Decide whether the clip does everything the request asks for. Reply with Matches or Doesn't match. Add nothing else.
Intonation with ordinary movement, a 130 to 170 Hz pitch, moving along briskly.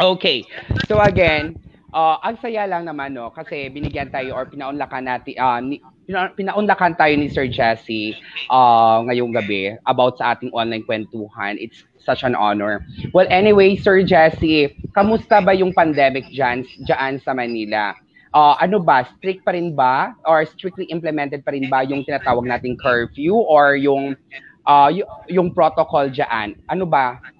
Doesn't match